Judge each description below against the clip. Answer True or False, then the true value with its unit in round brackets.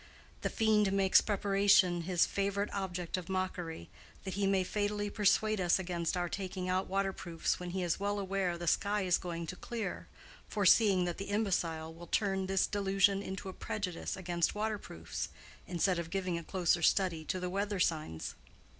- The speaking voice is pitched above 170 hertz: True (190 Hz)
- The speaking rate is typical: True (170 wpm)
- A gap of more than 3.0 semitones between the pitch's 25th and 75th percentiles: False (2.4 semitones)